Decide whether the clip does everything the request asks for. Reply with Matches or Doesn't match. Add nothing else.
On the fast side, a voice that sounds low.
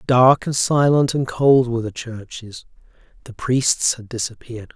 Doesn't match